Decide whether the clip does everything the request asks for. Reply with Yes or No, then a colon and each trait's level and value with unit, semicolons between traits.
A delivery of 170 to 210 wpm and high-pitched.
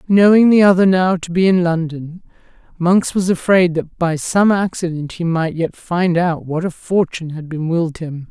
No: average, 195 wpm; medium, 175 Hz